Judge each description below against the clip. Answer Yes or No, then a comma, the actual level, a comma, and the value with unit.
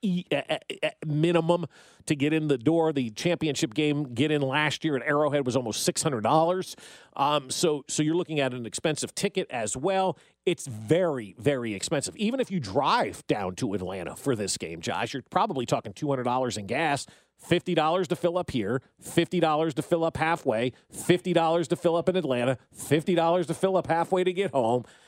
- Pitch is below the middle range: No, medium, 155 Hz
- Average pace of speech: Yes, average, 175 wpm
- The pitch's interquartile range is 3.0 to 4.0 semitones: No, average, 4.6 semitones